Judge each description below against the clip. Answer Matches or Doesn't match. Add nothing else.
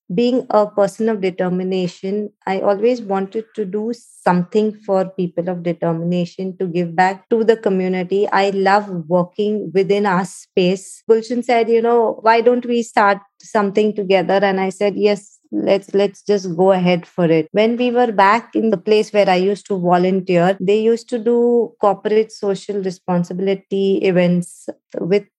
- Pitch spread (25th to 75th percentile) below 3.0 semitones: Matches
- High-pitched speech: Matches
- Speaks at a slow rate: Doesn't match